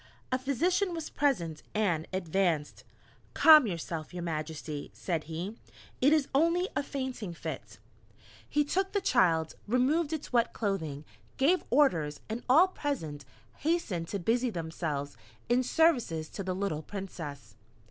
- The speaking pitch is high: Yes, high, 200 Hz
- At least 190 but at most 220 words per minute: No, slow, 135 wpm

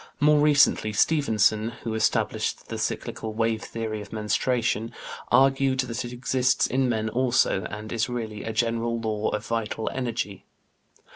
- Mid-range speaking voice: No, low, 115 Hz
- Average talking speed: Yes, average, 145 wpm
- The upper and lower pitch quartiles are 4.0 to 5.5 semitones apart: No, average, 2.7 semitones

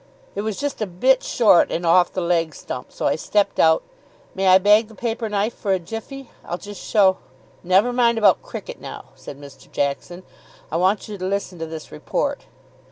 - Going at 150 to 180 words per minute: No, fast, 205 wpm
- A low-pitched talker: No, high, 190 Hz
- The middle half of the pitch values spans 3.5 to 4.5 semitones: Yes, average, 4.1 semitones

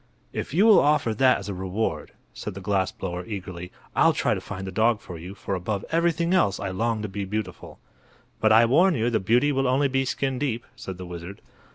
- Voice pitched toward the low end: Yes, low, 110 Hz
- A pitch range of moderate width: No, wide, 5.8 semitones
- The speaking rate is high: Yes, fast, 225 wpm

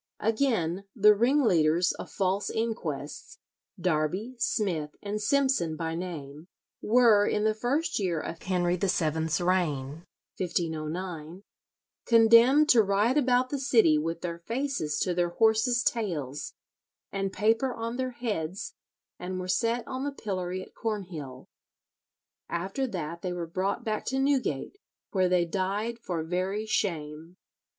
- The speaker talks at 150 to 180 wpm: No, slow, 135 wpm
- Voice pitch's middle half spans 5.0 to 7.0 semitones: Yes, wide, 5.5 semitones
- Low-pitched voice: No, high, 190 Hz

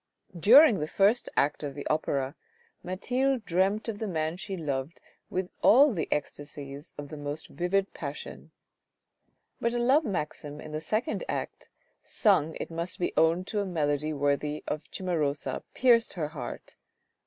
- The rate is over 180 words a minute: No, average, 155 wpm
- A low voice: No, medium, 170 Hz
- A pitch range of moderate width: No, wide, 5.8 semitones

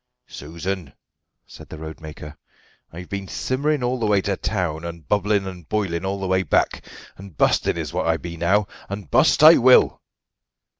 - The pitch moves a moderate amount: Yes, average, 3.7 semitones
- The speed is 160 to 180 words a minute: Yes, average, 170 wpm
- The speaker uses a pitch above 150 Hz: No, very low, 95 Hz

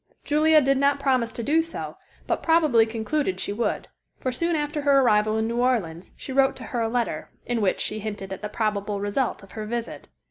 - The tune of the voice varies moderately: Yes, average, 4.8 semitones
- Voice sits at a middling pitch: No, high, 235 Hz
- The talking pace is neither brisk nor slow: No, fast, 215 wpm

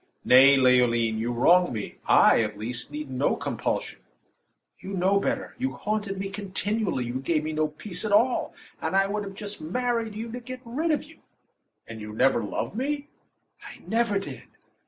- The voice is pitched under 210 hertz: Yes, high, 190 Hz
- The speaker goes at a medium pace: Yes, average, 180 wpm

